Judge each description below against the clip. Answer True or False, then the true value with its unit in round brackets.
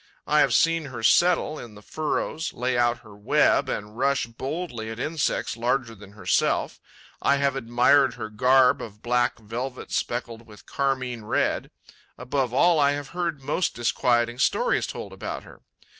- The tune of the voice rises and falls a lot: False (3.4 semitones)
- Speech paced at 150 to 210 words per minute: True (160 wpm)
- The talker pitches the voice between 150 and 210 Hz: False (125 Hz)